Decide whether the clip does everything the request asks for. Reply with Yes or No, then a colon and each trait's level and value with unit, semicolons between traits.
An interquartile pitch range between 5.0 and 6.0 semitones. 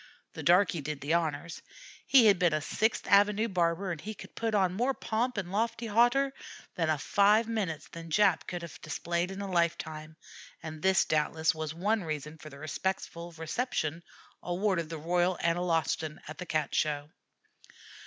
No: average, 4.4 semitones